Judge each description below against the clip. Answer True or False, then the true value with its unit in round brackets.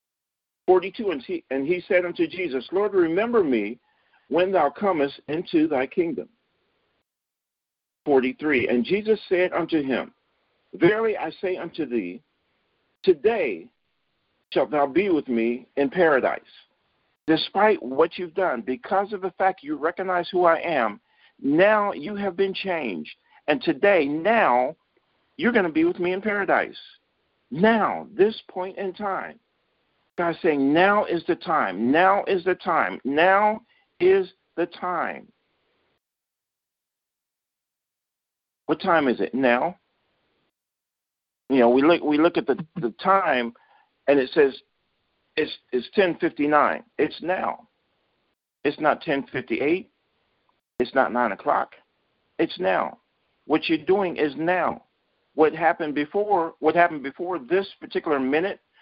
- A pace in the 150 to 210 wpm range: False (135 wpm)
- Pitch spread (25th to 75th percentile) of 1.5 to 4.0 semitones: False (5.1 semitones)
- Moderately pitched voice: True (180 Hz)